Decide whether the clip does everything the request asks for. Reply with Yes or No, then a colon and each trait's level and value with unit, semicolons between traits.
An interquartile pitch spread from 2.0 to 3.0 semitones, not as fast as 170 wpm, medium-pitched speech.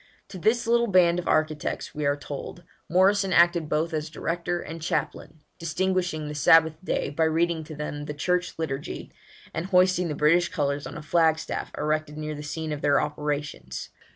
No: average, 2.7 semitones; average, 180 wpm; medium, 160 Hz